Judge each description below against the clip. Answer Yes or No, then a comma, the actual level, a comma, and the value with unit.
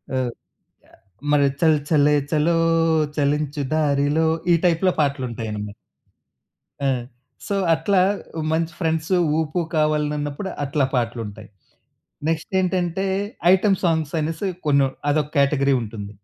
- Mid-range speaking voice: Yes, medium, 150 Hz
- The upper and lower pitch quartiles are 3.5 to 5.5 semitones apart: No, average, 2.7 semitones